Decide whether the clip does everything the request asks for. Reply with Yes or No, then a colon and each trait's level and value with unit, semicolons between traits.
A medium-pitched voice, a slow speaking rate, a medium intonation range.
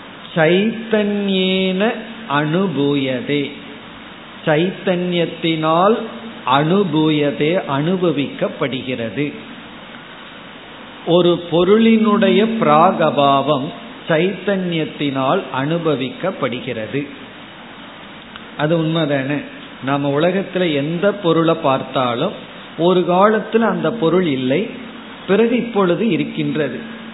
No: medium, 175 Hz; slow, 55 wpm; wide, 6.0 semitones